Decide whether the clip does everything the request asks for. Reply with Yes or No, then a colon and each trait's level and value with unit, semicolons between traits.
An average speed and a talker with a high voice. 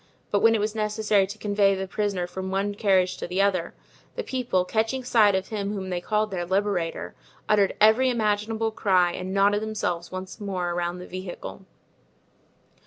Yes: average, 175 wpm; high, 200 Hz